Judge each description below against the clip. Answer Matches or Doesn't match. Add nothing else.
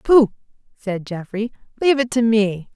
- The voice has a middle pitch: Doesn't match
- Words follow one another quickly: Doesn't match